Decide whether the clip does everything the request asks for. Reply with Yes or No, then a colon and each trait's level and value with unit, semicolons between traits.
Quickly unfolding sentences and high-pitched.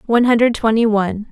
No: average, 185 wpm; high, 225 Hz